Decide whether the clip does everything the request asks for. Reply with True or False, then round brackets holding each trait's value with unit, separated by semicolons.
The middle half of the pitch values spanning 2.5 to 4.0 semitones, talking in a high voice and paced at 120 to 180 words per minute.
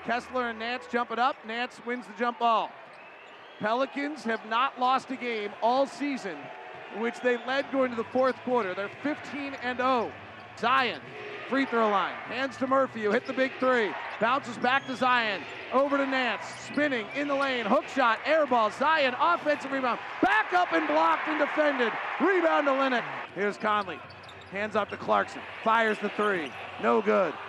True (3.3 semitones; 250 Hz; 175 wpm)